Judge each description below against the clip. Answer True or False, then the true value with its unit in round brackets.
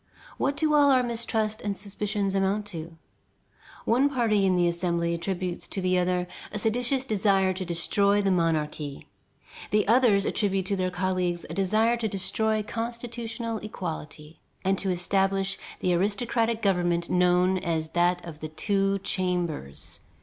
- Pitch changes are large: False (3.6 semitones)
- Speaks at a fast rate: False (150 wpm)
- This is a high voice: True (195 Hz)